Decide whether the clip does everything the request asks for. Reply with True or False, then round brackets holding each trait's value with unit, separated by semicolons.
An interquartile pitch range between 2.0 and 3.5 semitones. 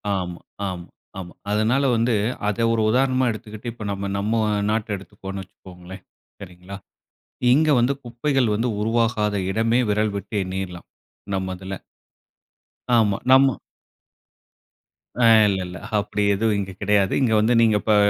True (3.1 semitones)